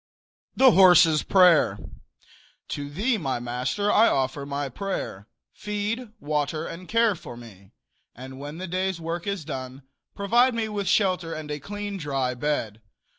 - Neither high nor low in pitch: Yes, medium, 165 Hz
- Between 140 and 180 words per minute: Yes, average, 150 wpm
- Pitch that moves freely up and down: Yes, wide, 6.7 semitones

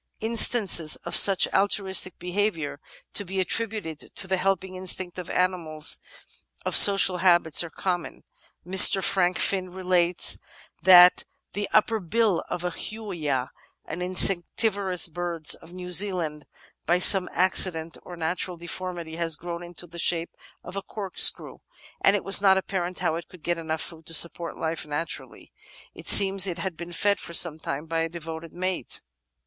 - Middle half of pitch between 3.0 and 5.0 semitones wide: No, narrow, 2.4 semitones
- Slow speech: No, average, 160 wpm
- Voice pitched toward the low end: No, medium, 180 Hz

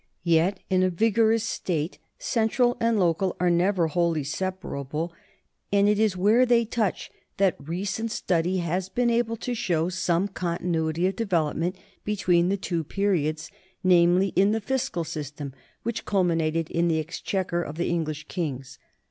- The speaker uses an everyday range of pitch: Yes, average, 3.7 semitones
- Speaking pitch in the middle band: Yes, medium, 180 Hz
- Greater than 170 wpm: No, average, 155 wpm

